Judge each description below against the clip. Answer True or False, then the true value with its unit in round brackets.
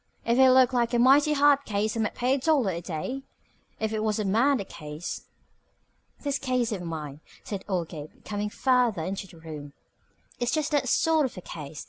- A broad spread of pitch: True (6.9 semitones)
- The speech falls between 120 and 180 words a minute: False (200 wpm)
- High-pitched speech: True (220 Hz)